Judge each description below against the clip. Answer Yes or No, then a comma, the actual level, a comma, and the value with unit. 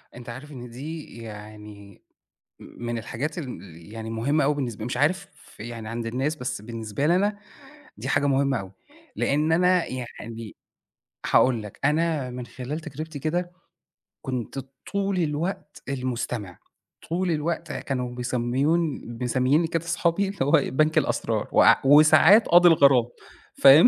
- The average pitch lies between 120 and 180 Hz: Yes, low, 135 Hz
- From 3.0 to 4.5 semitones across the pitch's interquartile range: No, average, 5.1 semitones